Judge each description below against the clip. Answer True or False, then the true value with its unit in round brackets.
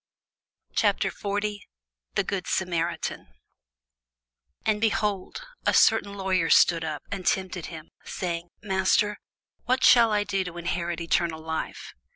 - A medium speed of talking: False (125 wpm)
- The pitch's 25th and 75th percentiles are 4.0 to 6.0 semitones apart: False (3.3 semitones)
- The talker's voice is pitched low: False (185 Hz)